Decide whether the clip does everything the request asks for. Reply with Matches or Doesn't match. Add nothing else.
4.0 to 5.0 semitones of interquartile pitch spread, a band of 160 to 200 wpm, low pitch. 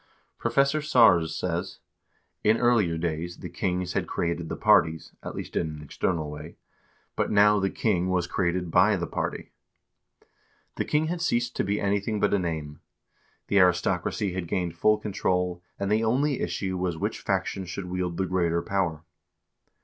Doesn't match